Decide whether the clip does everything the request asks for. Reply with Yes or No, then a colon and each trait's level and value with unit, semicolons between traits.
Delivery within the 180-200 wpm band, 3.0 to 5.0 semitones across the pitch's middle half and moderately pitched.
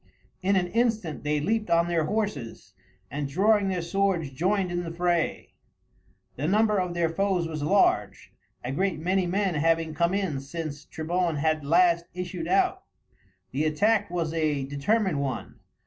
No: average, 160 wpm; average, 4.0 semitones; medium, 170 Hz